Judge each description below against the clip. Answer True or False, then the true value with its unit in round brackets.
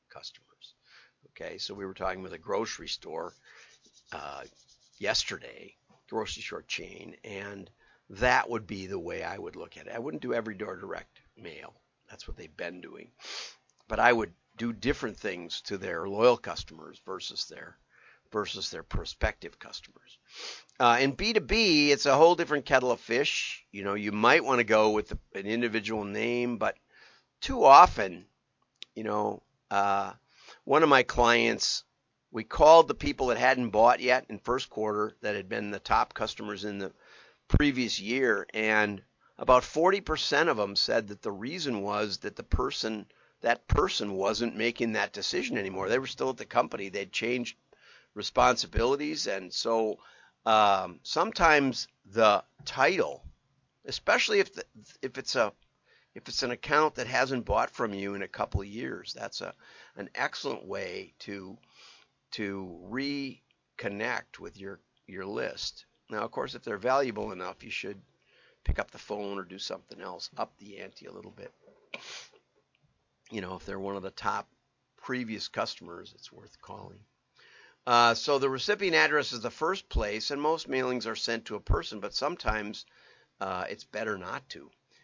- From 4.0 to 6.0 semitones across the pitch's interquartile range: True (4.6 semitones)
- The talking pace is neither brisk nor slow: True (165 wpm)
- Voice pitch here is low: True (115 Hz)